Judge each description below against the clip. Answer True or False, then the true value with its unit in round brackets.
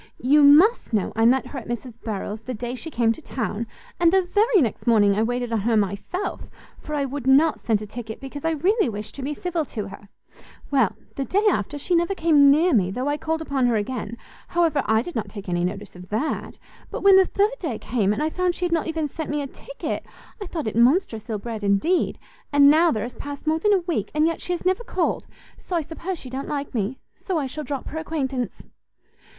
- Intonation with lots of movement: True (6.4 semitones)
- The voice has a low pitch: False (275 Hz)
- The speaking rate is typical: False (240 wpm)